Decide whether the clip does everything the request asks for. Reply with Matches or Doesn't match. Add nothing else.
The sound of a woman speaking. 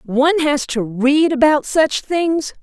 Matches